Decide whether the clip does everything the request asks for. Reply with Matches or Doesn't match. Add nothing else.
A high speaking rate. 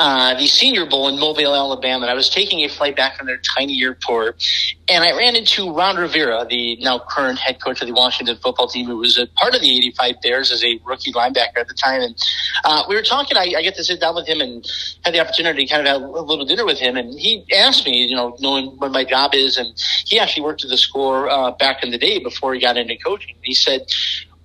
Matches